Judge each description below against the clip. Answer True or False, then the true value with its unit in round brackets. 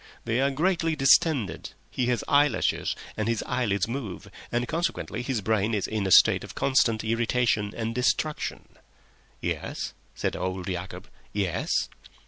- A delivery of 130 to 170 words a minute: True (140 wpm)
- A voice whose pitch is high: False (115 Hz)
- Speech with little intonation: False (4.5 semitones)